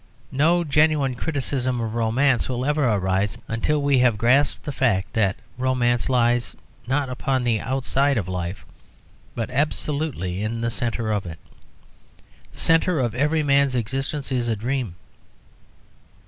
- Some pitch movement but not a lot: Yes, average, 3.6 semitones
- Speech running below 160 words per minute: Yes, average, 145 wpm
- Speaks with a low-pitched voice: Yes, low, 125 Hz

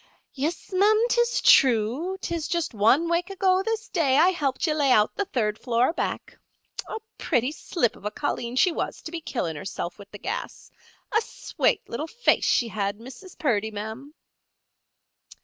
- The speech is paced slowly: No, average, 165 wpm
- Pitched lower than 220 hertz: No, very high, 290 Hz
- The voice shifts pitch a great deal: Yes, wide, 7.9 semitones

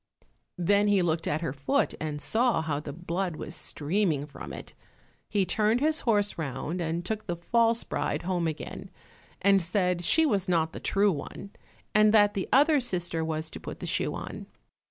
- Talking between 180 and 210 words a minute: Yes, average, 185 wpm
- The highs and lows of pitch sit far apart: No, average, 4.5 semitones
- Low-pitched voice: No, medium, 180 Hz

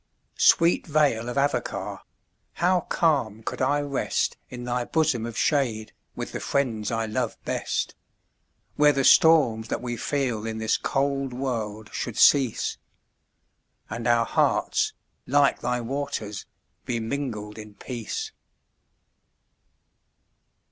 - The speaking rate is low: Yes, slow, 120 wpm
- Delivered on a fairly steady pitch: No, average, 4.1 semitones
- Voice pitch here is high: No, low, 125 Hz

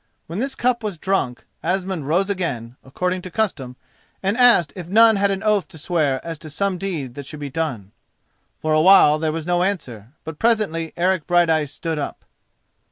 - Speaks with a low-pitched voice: No, medium, 170 Hz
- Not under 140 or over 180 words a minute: No, average, 190 wpm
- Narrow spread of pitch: No, average, 4.4 semitones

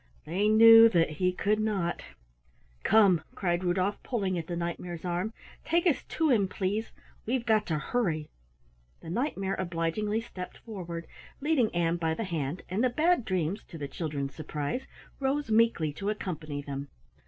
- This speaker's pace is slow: No, average, 165 wpm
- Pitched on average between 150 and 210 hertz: Yes, medium, 185 Hz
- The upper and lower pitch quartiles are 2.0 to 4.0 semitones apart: No, average, 4.9 semitones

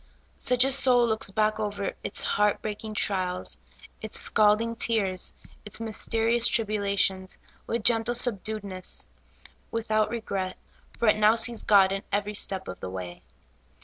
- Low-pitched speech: No, high, 215 Hz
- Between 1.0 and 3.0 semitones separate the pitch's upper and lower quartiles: Yes, narrow, 2.5 semitones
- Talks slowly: No, average, 145 wpm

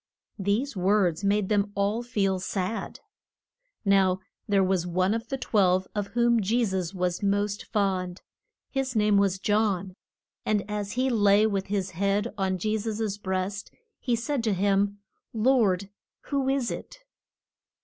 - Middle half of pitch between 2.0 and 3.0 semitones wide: Yes, narrow, 2.5 semitones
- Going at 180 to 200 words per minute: No, average, 150 wpm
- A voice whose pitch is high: Yes, high, 200 Hz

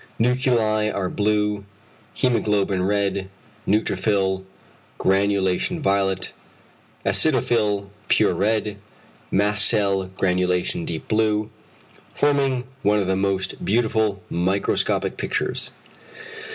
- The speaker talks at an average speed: No, slow, 85 wpm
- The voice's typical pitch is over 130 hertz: No, low, 100 Hz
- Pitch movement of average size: No, narrow, 2.1 semitones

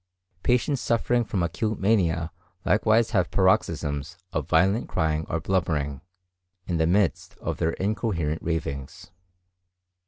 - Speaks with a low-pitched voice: Yes, very low, 90 Hz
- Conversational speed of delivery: No, slow, 120 wpm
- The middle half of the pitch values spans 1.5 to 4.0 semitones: No, average, 5.1 semitones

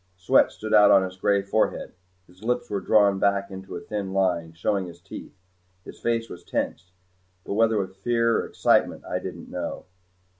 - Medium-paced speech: Yes, average, 185 wpm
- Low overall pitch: Yes, low, 100 Hz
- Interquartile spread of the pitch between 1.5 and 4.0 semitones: Yes, narrow, 2.5 semitones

